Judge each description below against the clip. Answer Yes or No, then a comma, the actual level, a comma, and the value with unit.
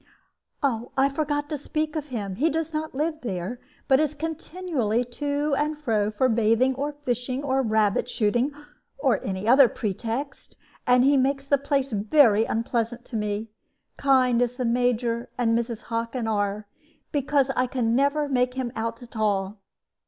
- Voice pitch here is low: No, very high, 250 Hz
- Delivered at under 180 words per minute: Yes, average, 160 wpm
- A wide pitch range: No, average, 3.8 semitones